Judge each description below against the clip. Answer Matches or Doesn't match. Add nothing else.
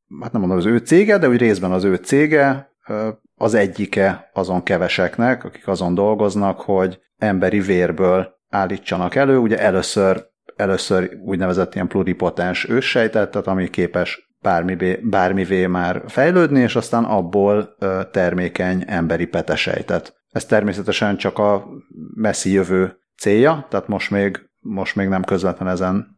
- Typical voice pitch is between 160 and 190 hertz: Doesn't match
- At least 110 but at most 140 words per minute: Matches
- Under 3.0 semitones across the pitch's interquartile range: Matches